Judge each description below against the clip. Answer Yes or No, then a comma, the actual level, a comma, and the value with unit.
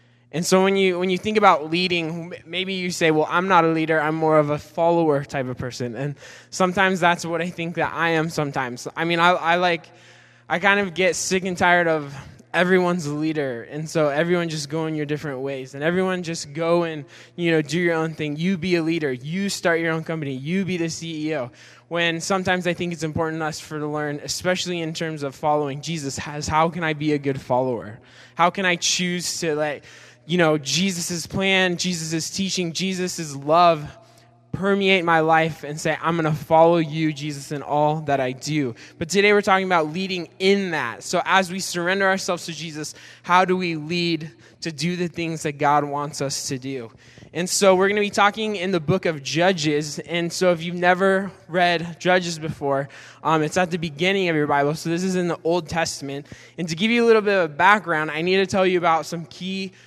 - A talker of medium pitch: Yes, medium, 165 Hz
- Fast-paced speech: Yes, fast, 220 wpm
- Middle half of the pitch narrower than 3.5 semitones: Yes, average, 3.1 semitones